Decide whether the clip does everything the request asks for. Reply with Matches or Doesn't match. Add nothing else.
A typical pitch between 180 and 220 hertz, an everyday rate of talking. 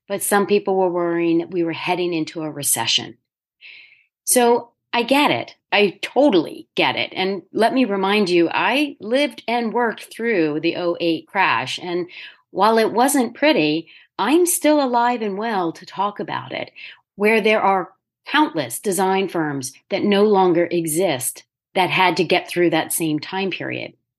Matches